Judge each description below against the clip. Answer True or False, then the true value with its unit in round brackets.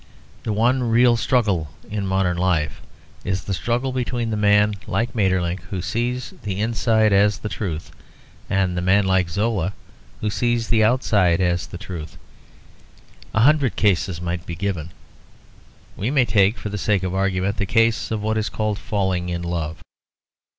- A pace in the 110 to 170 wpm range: True (165 wpm)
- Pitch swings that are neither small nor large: True (3.6 semitones)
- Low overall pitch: True (100 Hz)